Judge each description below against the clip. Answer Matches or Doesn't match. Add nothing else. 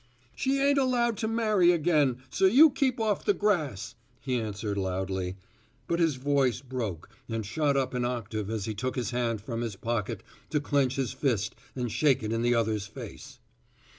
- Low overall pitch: Matches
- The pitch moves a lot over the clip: Matches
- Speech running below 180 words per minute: Doesn't match